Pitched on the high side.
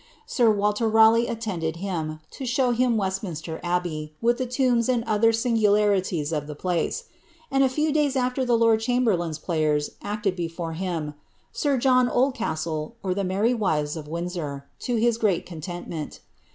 Yes: high, 205 Hz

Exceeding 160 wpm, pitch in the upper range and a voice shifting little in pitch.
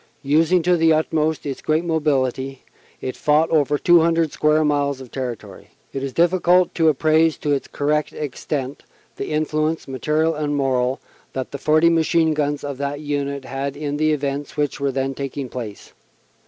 No: average, 170 wpm; medium, 145 Hz; narrow, 2.3 semitones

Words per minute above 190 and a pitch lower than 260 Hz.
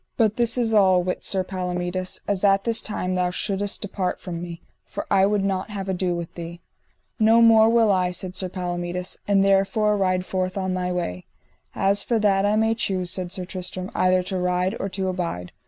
Yes: average, 200 wpm; high, 190 Hz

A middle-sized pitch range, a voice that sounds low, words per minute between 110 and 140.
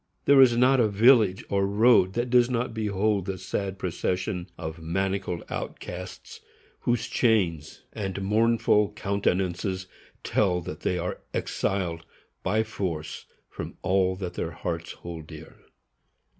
Yes: average, 3.5 semitones; very low, 95 Hz; slow, 135 wpm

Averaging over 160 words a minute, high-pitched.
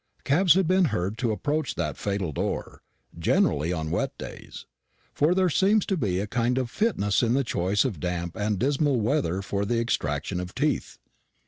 No: average, 185 wpm; low, 115 Hz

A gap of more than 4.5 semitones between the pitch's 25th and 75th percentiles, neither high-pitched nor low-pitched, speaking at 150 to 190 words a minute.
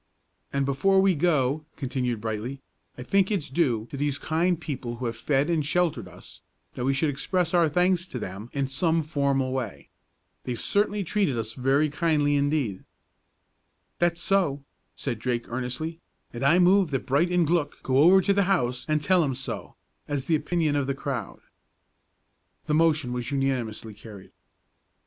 Yes: average, 5.0 semitones; medium, 145 Hz; average, 170 wpm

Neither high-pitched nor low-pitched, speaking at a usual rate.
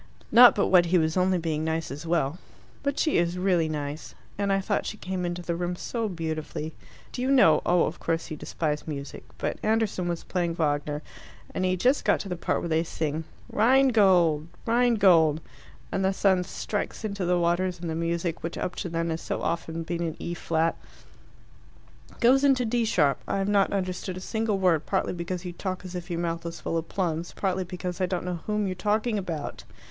No: medium, 175 Hz; fast, 210 wpm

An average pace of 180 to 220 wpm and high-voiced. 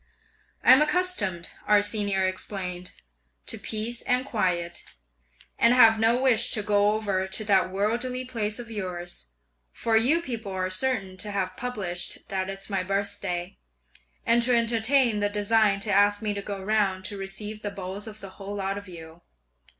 No: average, 165 wpm; high, 205 Hz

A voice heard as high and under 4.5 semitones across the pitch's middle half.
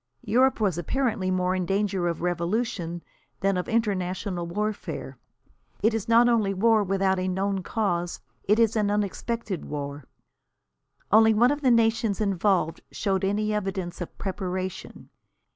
Yes: high, 195 Hz; average, 3.2 semitones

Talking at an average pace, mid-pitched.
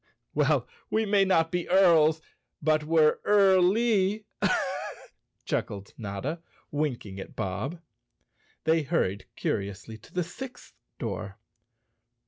No: slow, 105 wpm; medium, 160 Hz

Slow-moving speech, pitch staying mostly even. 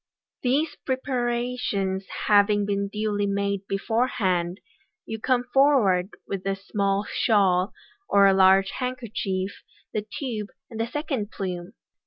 No: slow, 115 wpm; average, 3.7 semitones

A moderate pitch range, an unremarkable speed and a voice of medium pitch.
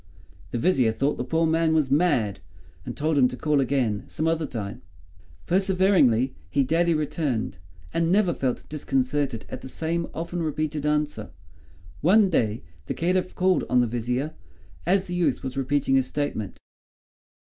Yes: average, 4.7 semitones; average, 160 wpm; medium, 150 Hz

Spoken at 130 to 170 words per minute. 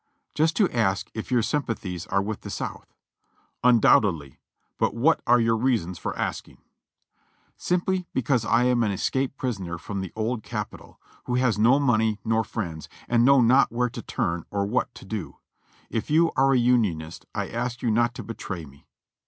No: average, 180 wpm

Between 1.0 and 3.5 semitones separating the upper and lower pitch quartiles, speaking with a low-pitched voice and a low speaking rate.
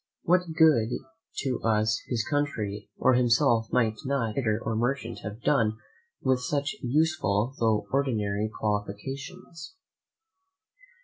No: average, 4.5 semitones; low, 125 Hz; slow, 115 wpm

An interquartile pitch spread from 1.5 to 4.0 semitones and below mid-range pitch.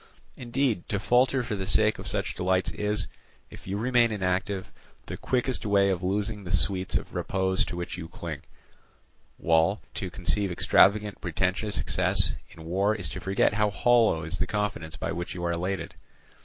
Yes: average, 2.8 semitones; low, 100 Hz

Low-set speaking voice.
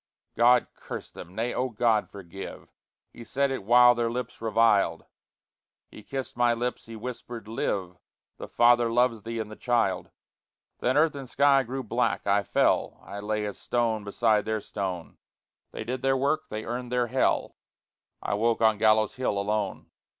Yes: low, 115 Hz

